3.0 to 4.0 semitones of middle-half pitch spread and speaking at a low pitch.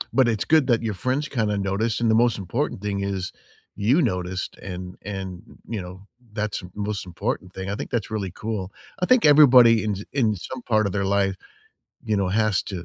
Yes: average, 3.4 semitones; low, 105 Hz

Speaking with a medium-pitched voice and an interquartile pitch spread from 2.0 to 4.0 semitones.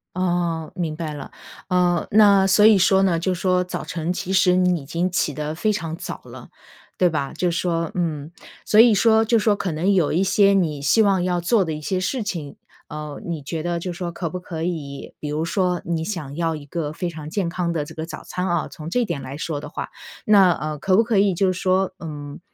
Yes: medium, 175 Hz; average, 3.1 semitones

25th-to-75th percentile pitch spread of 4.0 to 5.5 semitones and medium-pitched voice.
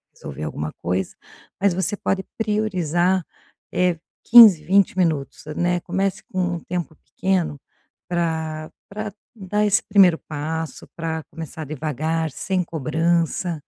No: average, 3.2 semitones; medium, 170 Hz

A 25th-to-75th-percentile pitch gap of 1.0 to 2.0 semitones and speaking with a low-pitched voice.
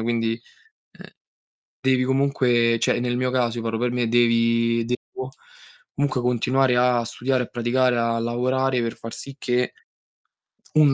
Yes: narrow, 1.7 semitones; low, 120 Hz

